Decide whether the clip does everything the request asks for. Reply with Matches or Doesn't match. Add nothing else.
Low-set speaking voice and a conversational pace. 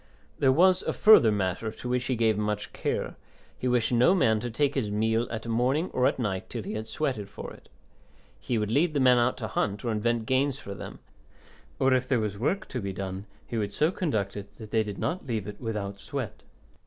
Doesn't match